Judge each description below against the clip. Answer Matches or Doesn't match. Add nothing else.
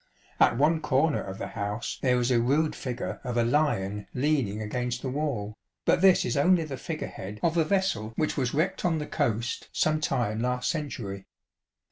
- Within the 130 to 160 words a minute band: Doesn't match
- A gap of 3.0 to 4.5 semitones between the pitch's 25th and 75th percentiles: Doesn't match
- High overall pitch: Doesn't match